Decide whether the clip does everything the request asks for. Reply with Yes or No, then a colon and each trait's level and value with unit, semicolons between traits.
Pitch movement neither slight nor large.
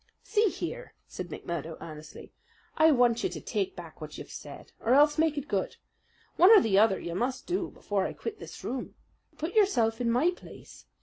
No: wide, 8.3 semitones